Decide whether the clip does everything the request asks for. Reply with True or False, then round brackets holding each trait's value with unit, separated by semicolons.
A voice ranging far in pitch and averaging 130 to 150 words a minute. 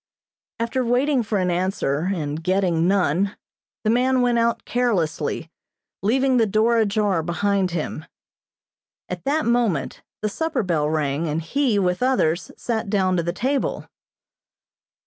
True (5.8 semitones; 140 wpm)